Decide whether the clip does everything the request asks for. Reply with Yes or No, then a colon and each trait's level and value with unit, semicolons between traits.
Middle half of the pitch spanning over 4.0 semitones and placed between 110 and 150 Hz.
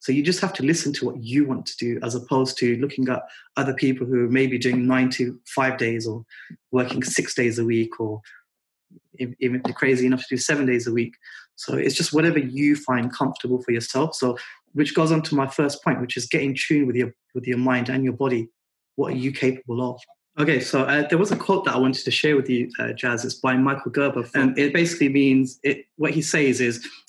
No: narrow, 2.4 semitones; low, 130 Hz